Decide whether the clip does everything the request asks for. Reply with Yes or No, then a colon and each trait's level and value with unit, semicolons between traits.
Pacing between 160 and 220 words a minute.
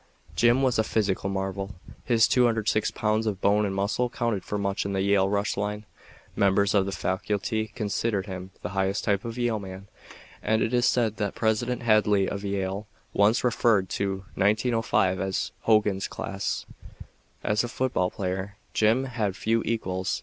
Yes: average, 165 wpm